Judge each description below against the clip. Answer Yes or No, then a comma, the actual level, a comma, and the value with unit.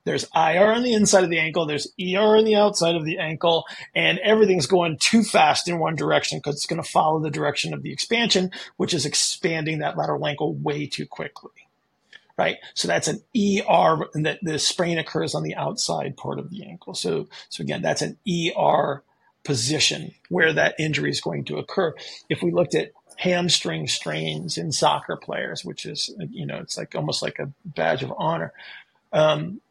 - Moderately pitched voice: Yes, medium, 170 Hz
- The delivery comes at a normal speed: Yes, average, 190 wpm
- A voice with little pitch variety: No, average, 3.9 semitones